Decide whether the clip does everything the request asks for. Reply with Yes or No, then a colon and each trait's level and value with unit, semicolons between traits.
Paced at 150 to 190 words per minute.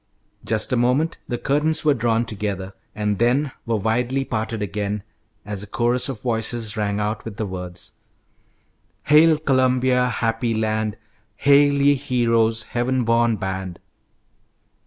No: slow, 135 wpm